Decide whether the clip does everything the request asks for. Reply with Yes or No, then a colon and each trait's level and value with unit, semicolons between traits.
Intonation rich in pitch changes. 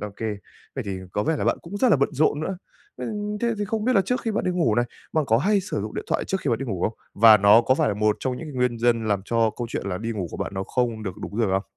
Yes: wide, 8.9 semitones